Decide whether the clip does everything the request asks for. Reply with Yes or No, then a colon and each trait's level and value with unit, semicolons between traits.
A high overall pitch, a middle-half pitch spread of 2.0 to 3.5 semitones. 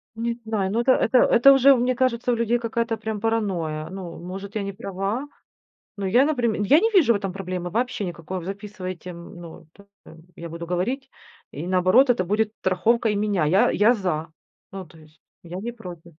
No: high, 200 Hz; average, 4.6 semitones